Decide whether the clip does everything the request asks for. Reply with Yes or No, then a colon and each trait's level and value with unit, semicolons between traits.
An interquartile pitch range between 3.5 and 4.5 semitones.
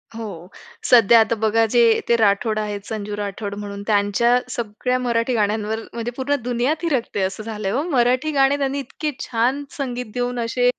No: average, 3.0 semitones